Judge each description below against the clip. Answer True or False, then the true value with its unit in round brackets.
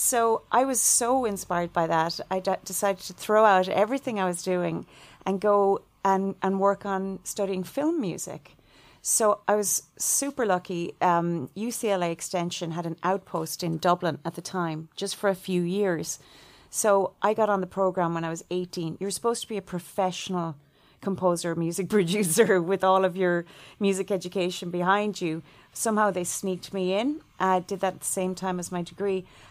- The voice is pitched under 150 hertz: False (190 Hz)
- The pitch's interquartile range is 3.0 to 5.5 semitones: False (2.5 semitones)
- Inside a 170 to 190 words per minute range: True (180 wpm)